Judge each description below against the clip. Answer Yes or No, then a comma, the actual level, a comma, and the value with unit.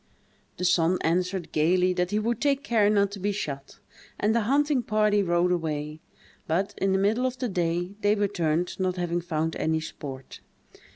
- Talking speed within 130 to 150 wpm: No, average, 180 wpm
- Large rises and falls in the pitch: No, average, 3.8 semitones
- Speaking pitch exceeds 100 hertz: Yes, medium, 185 Hz